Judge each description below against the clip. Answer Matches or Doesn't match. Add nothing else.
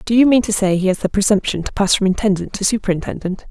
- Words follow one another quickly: Matches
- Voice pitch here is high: Matches